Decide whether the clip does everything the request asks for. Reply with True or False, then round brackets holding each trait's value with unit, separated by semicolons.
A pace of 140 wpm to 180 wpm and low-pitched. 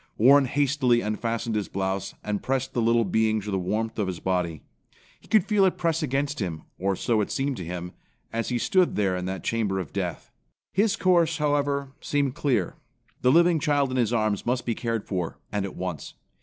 False (205 wpm; 115 Hz)